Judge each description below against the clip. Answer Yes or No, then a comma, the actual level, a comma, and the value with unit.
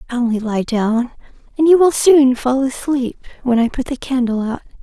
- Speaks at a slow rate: No, average, 185 wpm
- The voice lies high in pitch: Yes, very high, 255 Hz